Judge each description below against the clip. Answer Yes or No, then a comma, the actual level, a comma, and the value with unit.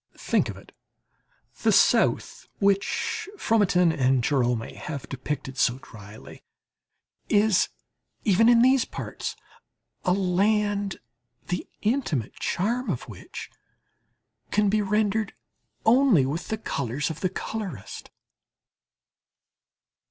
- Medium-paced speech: No, slow, 105 wpm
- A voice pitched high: Yes, high, 195 Hz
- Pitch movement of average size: No, wide, 7.4 semitones